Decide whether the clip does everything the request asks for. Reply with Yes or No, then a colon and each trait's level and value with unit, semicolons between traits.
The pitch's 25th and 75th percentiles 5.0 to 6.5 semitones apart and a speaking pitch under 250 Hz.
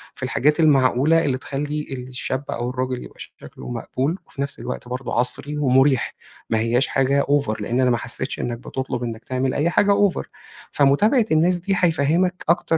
No: average, 3.8 semitones; low, 135 Hz